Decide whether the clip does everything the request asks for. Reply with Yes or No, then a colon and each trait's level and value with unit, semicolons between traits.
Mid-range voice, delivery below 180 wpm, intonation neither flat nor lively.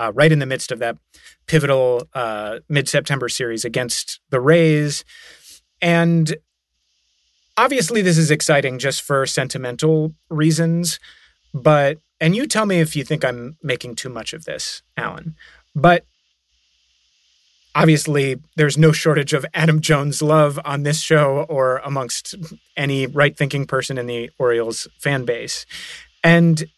Yes: medium, 145 Hz; average, 140 wpm; average, 4.0 semitones